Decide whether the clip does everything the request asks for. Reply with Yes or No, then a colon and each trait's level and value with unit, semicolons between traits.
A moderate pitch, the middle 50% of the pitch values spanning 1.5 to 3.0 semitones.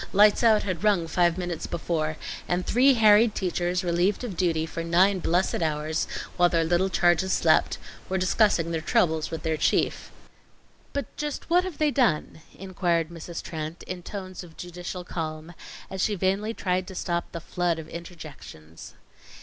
Yes: medium, 175 Hz; average, 2.7 semitones